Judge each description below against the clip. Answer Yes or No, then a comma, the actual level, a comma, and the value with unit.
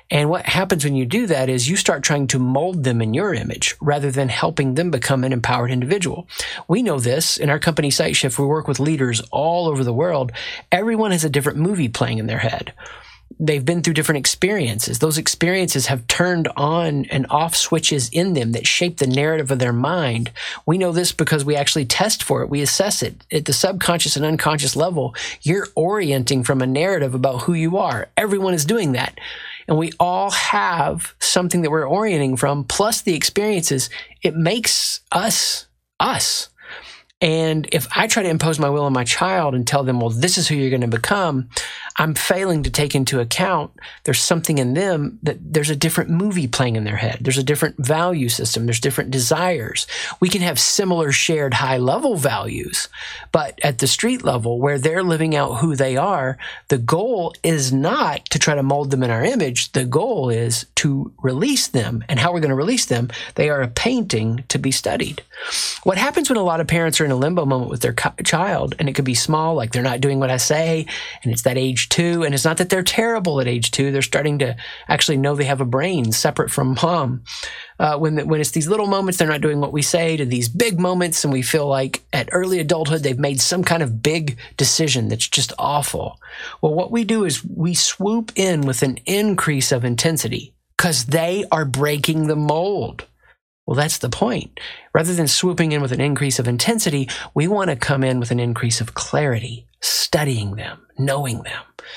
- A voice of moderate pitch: Yes, medium, 150 Hz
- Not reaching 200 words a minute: No, fast, 205 wpm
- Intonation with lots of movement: No, average, 4.5 semitones